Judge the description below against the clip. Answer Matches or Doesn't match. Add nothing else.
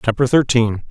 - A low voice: Matches